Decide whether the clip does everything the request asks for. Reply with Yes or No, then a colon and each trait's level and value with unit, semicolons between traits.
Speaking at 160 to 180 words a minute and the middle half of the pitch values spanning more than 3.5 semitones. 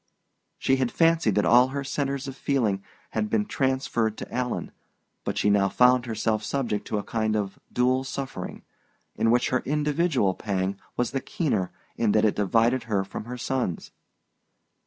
Yes: average, 170 wpm; average, 3.9 semitones